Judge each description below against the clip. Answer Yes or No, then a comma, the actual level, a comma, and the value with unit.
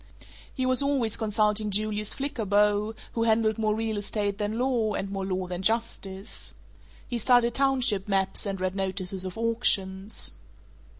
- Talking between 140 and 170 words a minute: Yes, average, 145 wpm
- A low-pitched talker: No, high, 210 Hz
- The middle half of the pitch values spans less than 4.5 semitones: Yes, average, 2.8 semitones